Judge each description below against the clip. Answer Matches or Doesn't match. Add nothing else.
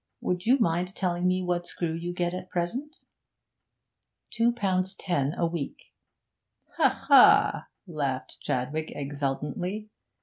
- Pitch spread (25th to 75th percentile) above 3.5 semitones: Doesn't match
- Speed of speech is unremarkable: Doesn't match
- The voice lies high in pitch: Doesn't match